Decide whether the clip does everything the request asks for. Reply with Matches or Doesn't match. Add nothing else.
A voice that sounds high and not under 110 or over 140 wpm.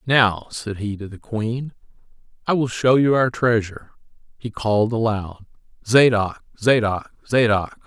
Doesn't match